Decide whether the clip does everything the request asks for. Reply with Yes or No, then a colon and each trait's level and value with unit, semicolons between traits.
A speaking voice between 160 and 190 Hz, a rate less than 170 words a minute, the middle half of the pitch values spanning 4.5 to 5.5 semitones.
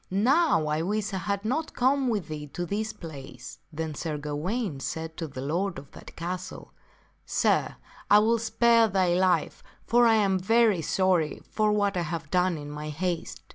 No: medium, 185 Hz; average, 185 wpm; average, 5.1 semitones